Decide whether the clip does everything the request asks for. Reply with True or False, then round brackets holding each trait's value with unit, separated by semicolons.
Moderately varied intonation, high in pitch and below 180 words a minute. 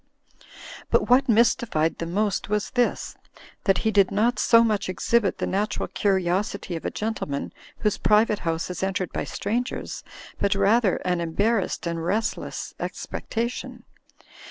True (3.6 semitones; 205 Hz; 145 wpm)